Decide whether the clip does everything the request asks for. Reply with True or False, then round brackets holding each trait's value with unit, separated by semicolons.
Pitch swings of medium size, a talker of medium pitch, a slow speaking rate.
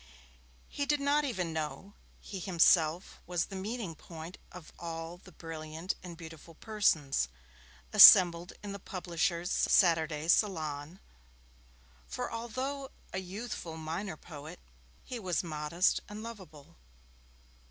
True (3.8 semitones; 175 Hz; 120 wpm)